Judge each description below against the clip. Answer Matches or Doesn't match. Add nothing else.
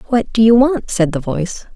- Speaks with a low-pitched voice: Doesn't match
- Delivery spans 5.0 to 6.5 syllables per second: Matches